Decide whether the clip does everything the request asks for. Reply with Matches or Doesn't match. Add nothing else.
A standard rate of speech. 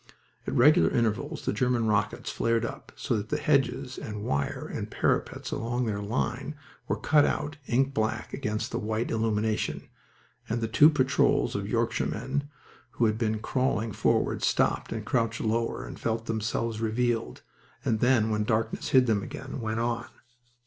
Matches